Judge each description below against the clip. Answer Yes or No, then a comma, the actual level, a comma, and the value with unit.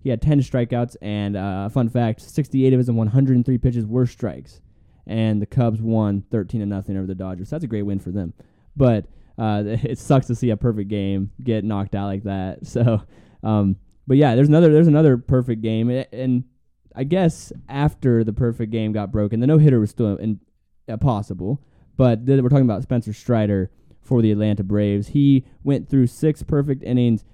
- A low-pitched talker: Yes, low, 115 Hz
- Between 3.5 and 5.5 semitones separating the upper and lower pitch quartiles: Yes, average, 4.0 semitones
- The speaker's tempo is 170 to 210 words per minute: Yes, average, 200 wpm